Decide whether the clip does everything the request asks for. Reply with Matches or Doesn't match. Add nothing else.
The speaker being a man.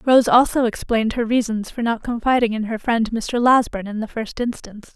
Doesn't match